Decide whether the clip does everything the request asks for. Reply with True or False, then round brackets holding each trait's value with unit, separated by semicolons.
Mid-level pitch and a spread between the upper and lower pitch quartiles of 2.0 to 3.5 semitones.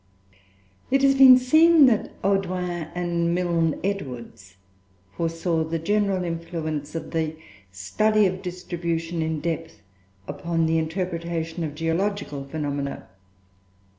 True (170 Hz; 2.9 semitones)